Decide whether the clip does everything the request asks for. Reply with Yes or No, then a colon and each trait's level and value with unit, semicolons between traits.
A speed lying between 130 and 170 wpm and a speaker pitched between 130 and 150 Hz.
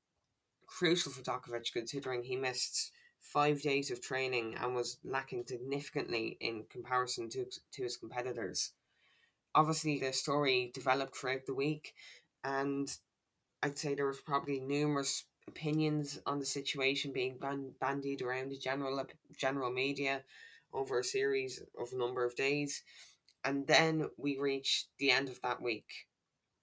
Yes: average, 140 wpm; low, 135 Hz